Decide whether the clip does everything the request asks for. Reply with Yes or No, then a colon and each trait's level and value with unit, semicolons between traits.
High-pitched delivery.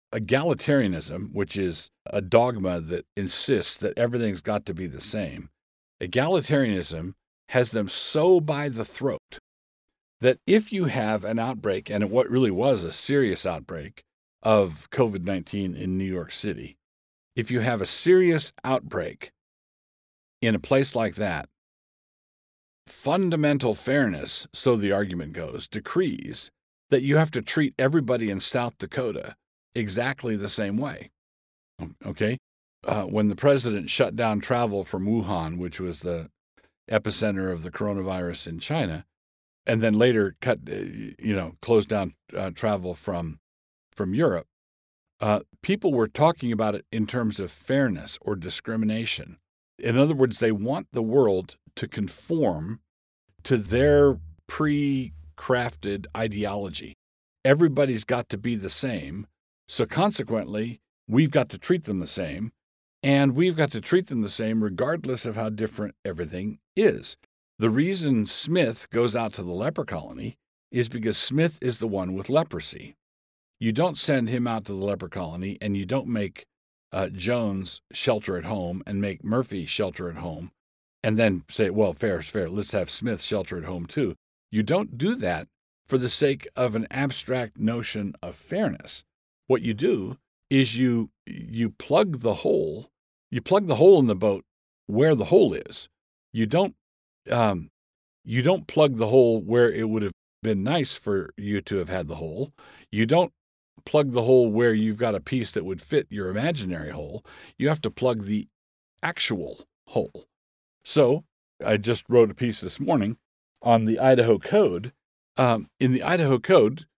No: low, 110 Hz